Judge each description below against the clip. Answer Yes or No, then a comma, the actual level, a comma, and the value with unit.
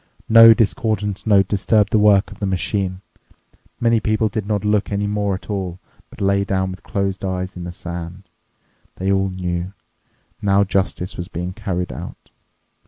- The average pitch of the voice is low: Yes, low, 100 Hz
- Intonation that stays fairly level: Yes, narrow, 2.0 semitones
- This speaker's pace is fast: No, average, 170 wpm